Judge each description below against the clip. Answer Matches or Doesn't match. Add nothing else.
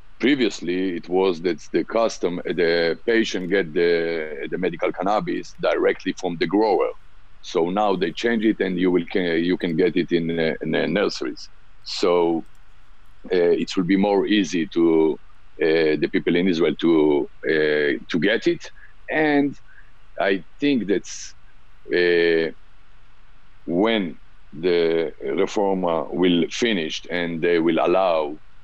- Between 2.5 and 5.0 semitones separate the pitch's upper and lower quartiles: Doesn't match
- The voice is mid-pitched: Doesn't match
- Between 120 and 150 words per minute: Matches